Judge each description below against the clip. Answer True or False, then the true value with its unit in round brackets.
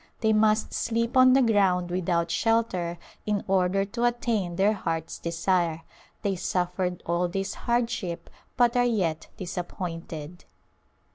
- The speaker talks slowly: True (130 wpm)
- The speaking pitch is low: False (190 Hz)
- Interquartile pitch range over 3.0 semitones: True (4.4 semitones)